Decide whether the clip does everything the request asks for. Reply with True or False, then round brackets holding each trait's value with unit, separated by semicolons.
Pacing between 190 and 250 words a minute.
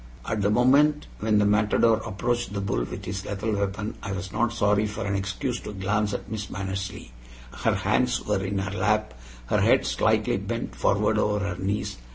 True (195 wpm)